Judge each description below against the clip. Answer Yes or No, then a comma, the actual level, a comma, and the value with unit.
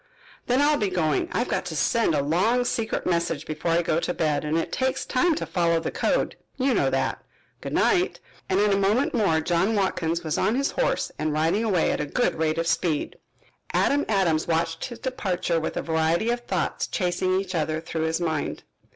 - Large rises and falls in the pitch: Yes, wide, 5.9 semitones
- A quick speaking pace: Yes, fast, 210 wpm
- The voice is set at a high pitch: No, medium, 175 Hz